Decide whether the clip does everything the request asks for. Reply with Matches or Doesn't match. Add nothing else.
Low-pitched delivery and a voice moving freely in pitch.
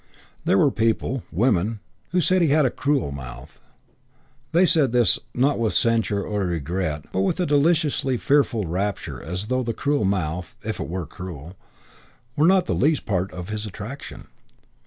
Matches